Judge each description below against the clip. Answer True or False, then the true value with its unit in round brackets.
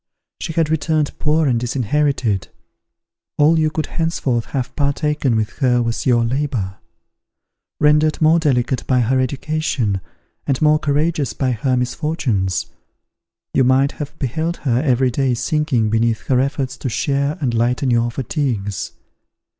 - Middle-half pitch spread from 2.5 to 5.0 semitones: True (3.9 semitones)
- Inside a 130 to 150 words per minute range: True (140 wpm)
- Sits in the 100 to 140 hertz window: True (135 Hz)